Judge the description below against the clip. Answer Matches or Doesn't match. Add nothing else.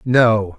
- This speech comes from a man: Matches